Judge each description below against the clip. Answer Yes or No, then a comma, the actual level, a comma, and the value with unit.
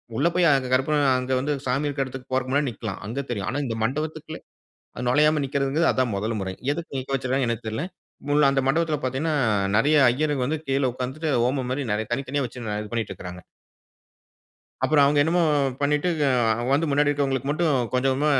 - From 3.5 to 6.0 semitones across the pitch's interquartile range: No, average, 2.8 semitones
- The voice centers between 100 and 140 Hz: Yes, low, 135 Hz